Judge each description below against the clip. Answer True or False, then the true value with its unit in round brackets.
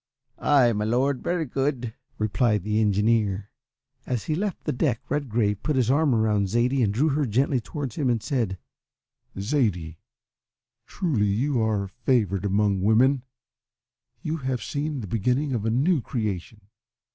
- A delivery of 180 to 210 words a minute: False (150 wpm)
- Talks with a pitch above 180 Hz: False (120 Hz)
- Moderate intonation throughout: True (4.7 semitones)